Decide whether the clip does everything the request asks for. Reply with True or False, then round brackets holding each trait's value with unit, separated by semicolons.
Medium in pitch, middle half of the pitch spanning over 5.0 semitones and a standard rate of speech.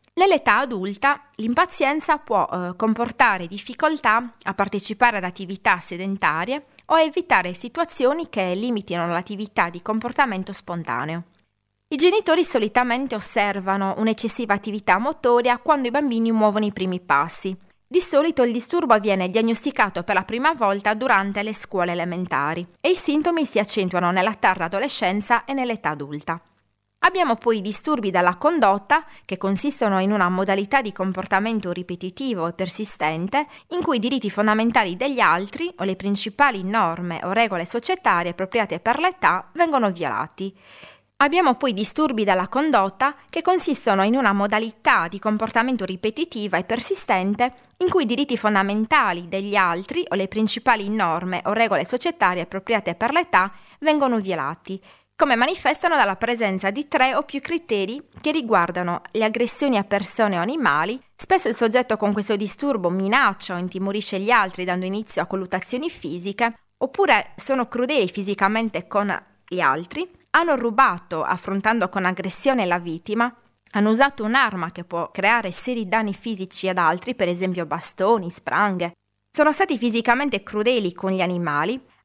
False (215 Hz; 5.6 semitones; 145 wpm)